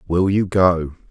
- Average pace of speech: Yes, average, 160 wpm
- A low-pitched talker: Yes, very low, 90 Hz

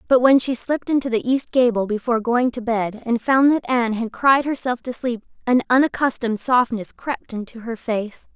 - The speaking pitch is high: Yes, high, 240 Hz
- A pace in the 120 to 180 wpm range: No, average, 200 wpm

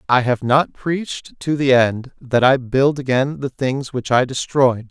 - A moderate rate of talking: Yes, average, 195 wpm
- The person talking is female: No, male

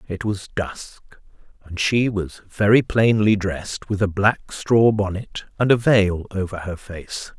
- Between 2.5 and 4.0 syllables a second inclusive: Yes, 3.9 syllables/s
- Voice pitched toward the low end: Yes, low, 100 Hz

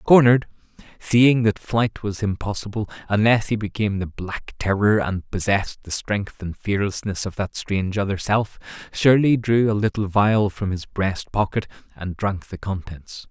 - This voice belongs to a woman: No, male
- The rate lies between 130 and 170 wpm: Yes, average, 160 wpm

